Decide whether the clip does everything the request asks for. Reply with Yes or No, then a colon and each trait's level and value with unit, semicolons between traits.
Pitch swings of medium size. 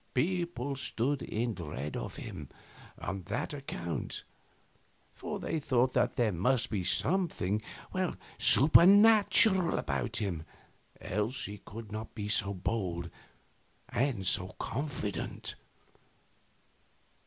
No: wide, 6.6 semitones